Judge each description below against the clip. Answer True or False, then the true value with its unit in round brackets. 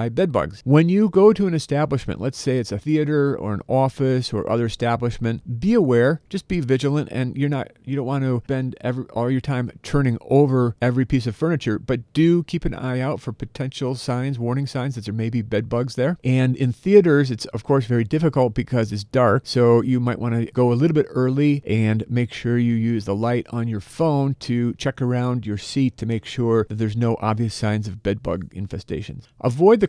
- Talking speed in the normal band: False (215 wpm)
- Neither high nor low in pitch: False (125 Hz)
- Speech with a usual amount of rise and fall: True (3.0 semitones)